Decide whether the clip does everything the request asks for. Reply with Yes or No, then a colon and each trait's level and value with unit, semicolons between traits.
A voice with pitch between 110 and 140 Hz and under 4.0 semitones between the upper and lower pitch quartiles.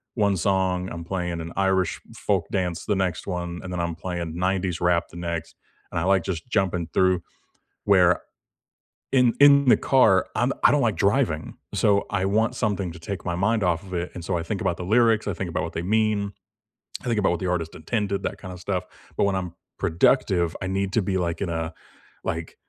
No: very low, 95 Hz; narrow, 2.6 semitones